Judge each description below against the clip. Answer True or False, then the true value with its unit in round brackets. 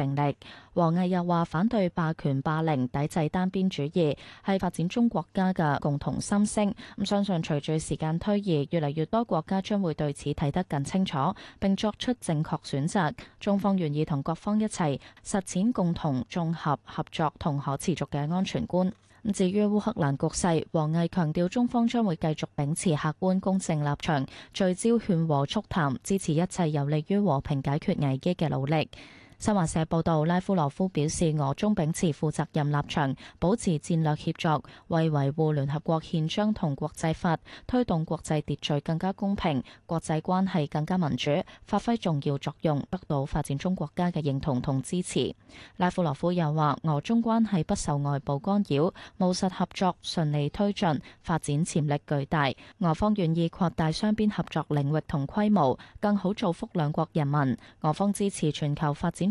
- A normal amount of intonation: True (4.1 semitones)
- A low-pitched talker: False (165 Hz)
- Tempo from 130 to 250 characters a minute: False (270 characters per minute)